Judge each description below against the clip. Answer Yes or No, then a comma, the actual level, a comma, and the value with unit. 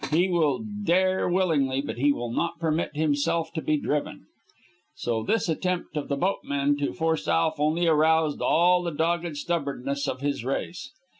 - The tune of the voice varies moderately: Yes, average, 3.3 semitones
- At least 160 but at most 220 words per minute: Yes, average, 165 wpm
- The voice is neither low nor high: Yes, medium, 160 Hz